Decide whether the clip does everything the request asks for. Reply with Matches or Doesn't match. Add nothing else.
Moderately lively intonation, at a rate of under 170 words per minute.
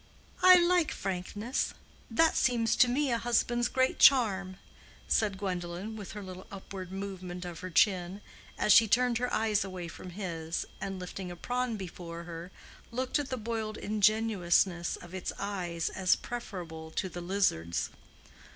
Matches